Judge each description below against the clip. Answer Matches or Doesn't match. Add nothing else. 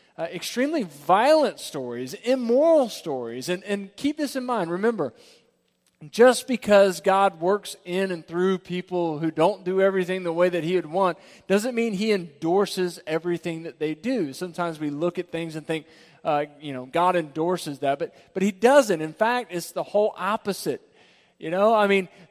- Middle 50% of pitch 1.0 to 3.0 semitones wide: Doesn't match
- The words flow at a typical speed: Matches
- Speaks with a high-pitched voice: Doesn't match